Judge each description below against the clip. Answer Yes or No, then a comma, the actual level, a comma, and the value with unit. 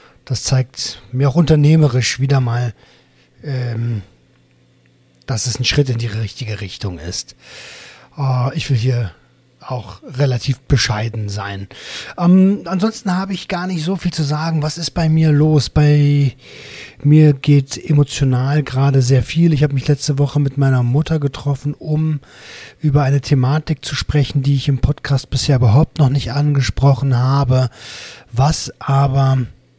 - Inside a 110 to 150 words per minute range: Yes, average, 145 wpm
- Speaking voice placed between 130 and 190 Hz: Yes, medium, 140 Hz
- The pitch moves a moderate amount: Yes, average, 3.0 semitones